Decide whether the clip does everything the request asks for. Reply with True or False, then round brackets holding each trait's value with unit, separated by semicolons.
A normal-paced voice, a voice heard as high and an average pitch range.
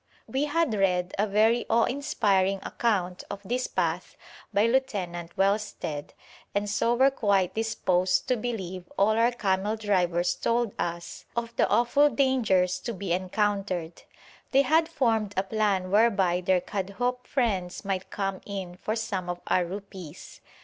True (150 wpm; 200 Hz; 4.1 semitones)